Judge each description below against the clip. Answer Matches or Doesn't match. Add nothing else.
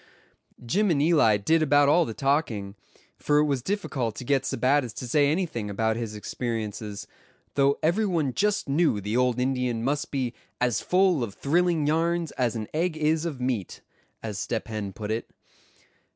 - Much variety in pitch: Matches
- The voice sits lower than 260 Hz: Matches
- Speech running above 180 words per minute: Doesn't match